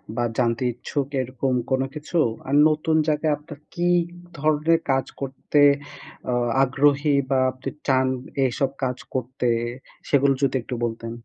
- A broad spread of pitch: No, narrow, 2.5 semitones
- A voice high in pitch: No, low, 135 Hz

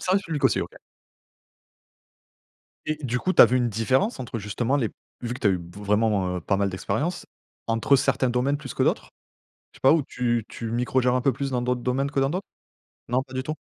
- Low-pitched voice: Yes, low, 125 Hz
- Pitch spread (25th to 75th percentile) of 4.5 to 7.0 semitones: No, average, 3.3 semitones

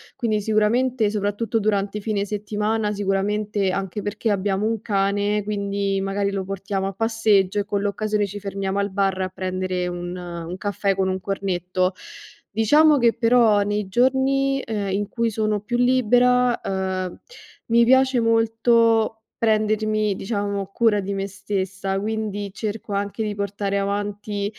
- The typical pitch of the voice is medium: No, high, 205 Hz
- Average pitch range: No, narrow, 2.1 semitones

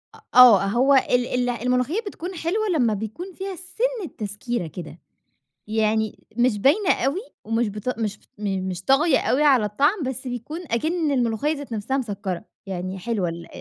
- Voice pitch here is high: Yes, high, 245 Hz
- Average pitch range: No, wide, 5.9 semitones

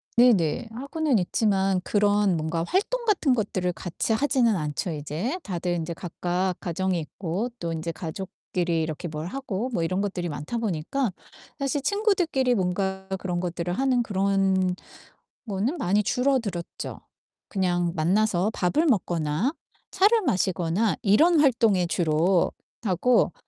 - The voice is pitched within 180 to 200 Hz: Yes, high, 190 Hz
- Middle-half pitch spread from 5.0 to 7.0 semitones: Yes, wide, 5.6 semitones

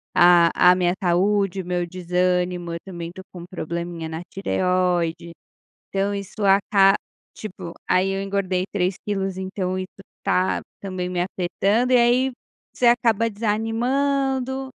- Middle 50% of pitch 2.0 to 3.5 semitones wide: Yes, narrow, 2.6 semitones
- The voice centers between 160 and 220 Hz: Yes, high, 190 Hz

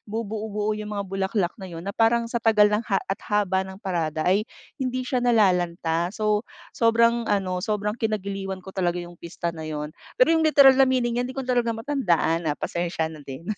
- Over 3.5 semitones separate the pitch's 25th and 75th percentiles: Yes, average, 4.7 semitones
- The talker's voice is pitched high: Yes, high, 205 Hz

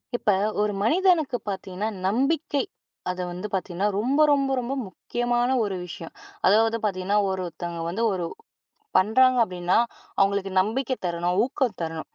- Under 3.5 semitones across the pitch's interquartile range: No, average, 5.3 semitones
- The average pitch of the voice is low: No, high, 205 Hz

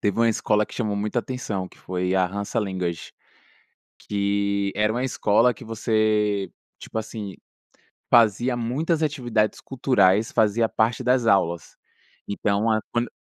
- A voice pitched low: Yes, low, 105 Hz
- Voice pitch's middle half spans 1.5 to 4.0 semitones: Yes, average, 2.9 semitones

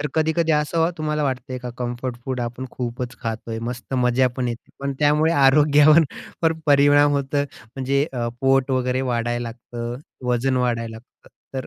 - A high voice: No, low, 130 Hz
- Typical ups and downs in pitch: Yes, average, 3.1 semitones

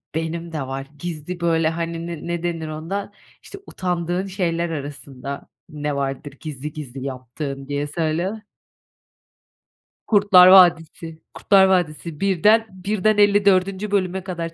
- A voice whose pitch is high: No, medium, 170 Hz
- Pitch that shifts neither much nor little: Yes, average, 3.7 semitones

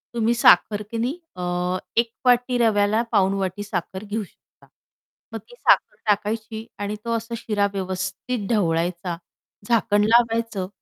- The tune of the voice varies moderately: Yes, average, 3.4 semitones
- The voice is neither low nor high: No, high, 210 Hz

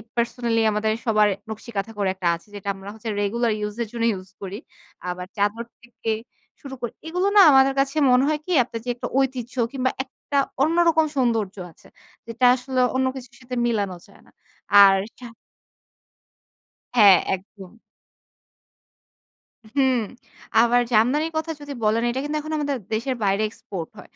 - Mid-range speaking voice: No, high, 235 Hz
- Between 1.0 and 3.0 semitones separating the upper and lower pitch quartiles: No, average, 4.2 semitones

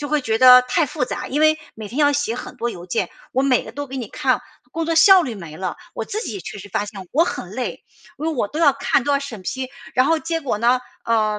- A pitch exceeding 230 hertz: Yes, very high, 255 Hz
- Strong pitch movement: No, average, 4.8 semitones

